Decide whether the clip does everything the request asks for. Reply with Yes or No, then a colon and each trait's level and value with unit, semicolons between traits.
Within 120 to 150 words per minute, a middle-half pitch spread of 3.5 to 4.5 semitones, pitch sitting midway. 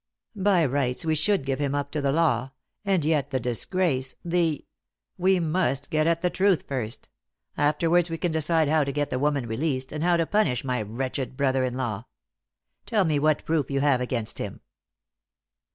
No: average, 190 wpm; average, 4.1 semitones; medium, 145 Hz